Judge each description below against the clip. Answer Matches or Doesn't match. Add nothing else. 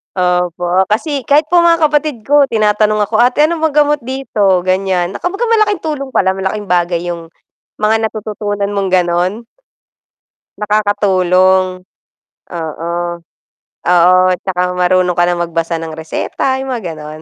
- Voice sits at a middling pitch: Doesn't match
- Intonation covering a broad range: Matches